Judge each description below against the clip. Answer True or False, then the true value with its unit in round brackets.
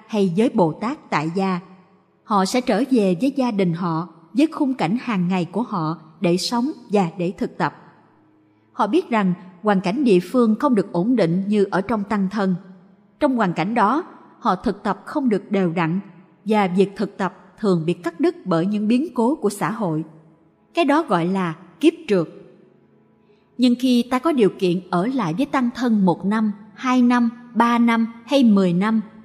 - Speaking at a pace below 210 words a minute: True (195 wpm)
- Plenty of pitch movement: False (5.0 semitones)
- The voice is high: True (200 Hz)